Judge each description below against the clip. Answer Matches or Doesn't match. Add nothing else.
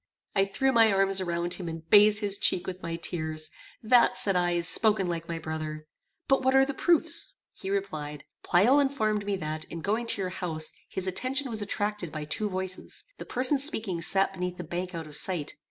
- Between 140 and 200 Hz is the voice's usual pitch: Matches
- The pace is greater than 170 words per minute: Matches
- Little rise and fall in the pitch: Doesn't match